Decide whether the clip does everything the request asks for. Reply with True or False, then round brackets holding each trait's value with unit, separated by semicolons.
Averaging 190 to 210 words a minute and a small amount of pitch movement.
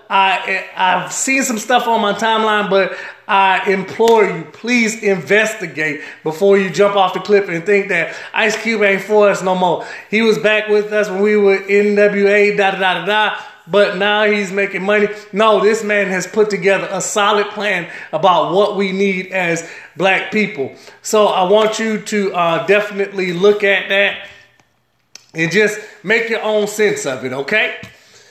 False (180 wpm; 1.9 semitones)